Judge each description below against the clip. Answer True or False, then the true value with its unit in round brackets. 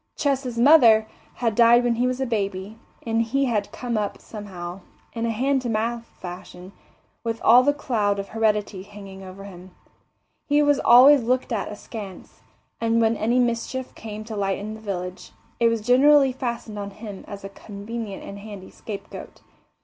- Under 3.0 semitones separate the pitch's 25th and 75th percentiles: False (3.3 semitones)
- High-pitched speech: True (225 Hz)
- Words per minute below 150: False (175 wpm)